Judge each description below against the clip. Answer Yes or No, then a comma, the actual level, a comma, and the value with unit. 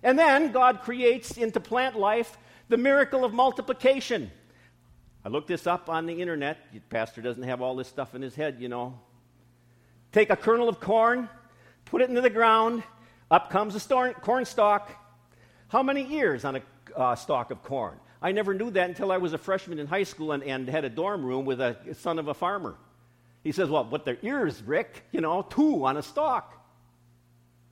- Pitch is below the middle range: No, medium, 170 Hz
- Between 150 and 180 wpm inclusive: No, average, 200 wpm